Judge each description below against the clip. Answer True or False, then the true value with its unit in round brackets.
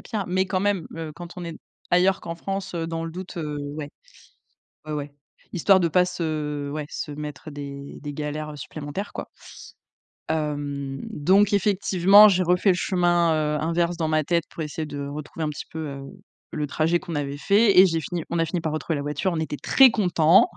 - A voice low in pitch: False (165 Hz)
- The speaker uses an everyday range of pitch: True (3.4 semitones)